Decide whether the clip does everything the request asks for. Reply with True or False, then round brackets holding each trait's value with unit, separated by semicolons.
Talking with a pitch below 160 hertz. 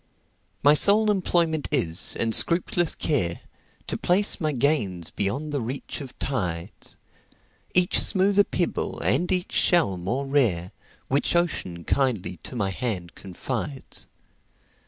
True (140 Hz)